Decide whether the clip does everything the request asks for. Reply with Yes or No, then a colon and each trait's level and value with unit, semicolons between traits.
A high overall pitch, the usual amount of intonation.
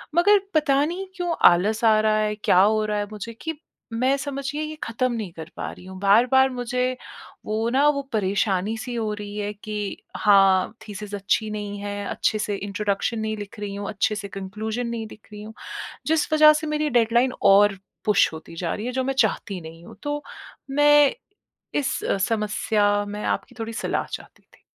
Yes: high, 215 Hz; average, 3.9 semitones